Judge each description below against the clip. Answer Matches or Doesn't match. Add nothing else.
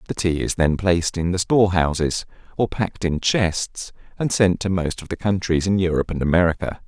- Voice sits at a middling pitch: Doesn't match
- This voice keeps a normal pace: Doesn't match